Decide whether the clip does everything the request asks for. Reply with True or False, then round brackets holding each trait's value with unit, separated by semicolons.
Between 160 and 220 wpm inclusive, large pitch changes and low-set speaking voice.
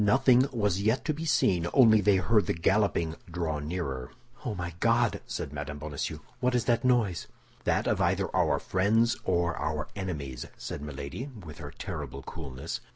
True (170 wpm; 7.2 semitones; 90 Hz)